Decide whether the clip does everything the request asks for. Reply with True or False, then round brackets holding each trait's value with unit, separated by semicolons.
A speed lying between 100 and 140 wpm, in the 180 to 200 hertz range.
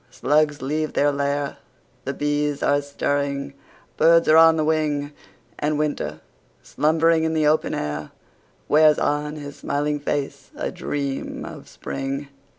False (135 wpm; 145 Hz)